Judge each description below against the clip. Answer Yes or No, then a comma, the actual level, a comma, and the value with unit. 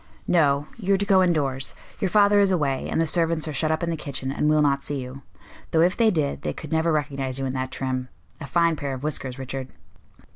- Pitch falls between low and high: Yes, medium, 150 Hz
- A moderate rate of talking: No, fast, 245 wpm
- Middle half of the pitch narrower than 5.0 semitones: Yes, average, 3.8 semitones